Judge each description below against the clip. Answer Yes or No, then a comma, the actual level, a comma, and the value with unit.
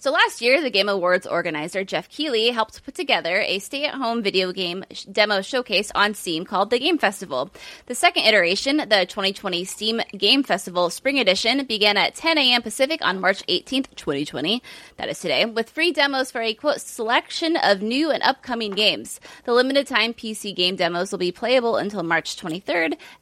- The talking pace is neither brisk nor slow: Yes, average, 190 wpm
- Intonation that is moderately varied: No, wide, 5.9 semitones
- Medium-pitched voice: No, high, 220 Hz